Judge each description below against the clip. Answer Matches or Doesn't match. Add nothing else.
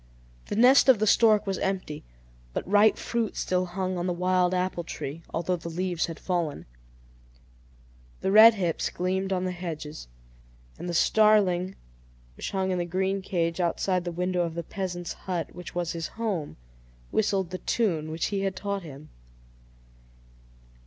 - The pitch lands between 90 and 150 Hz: Doesn't match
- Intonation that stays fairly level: Matches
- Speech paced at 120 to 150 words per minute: Doesn't match